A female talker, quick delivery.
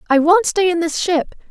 Yes: female; fast, 240 wpm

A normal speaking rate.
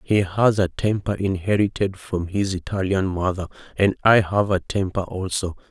Yes: average, 160 wpm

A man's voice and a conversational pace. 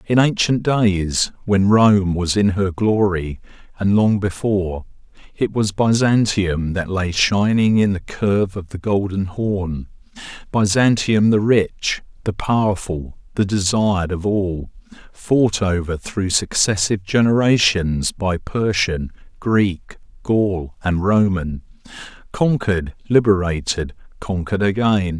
No: male; slow, 115 wpm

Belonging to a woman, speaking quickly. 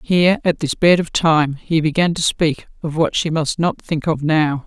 Yes: female; fast, 230 wpm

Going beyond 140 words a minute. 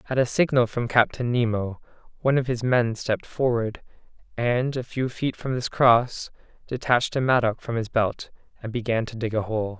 Yes: average, 190 wpm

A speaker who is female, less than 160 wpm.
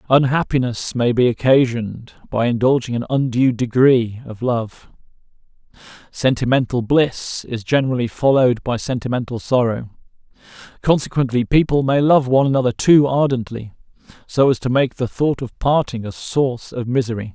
No: male; slow, 135 wpm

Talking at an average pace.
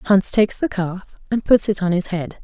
No: fast, 245 wpm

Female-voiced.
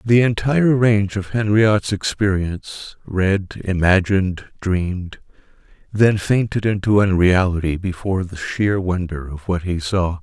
No: male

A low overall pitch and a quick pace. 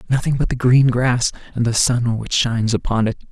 Yes: low, 120 Hz; fast, 215 wpm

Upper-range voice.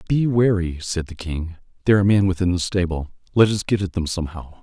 No: very low, 95 Hz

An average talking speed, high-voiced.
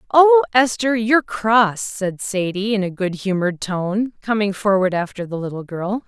Yes: average, 170 wpm; high, 205 Hz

